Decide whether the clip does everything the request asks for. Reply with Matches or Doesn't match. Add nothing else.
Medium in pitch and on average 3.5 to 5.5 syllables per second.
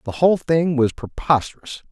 Matches